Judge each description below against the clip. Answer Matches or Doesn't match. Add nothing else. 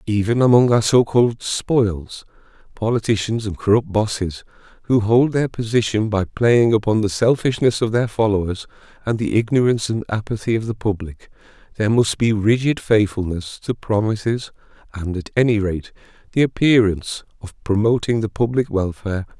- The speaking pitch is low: Matches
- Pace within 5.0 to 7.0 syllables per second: Matches